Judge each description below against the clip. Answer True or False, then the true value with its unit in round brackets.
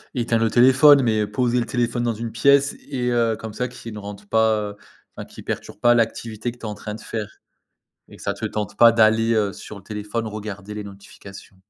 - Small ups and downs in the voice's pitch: True (2.3 semitones)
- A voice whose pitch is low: True (110 Hz)